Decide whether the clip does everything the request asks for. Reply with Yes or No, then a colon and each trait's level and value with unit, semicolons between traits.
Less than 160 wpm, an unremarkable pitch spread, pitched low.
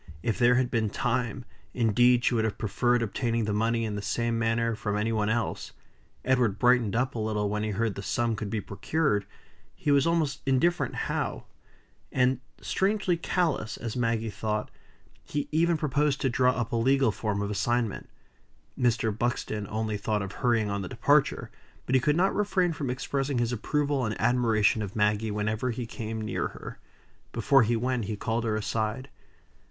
No: average, 180 wpm; average, 3.1 semitones; low, 115 Hz